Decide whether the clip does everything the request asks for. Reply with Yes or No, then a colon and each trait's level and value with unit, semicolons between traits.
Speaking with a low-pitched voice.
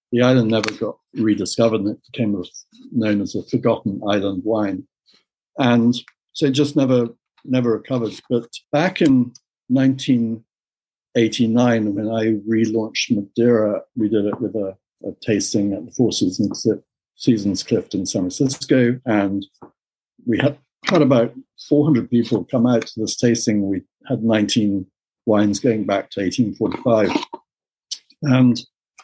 Yes: low, 115 Hz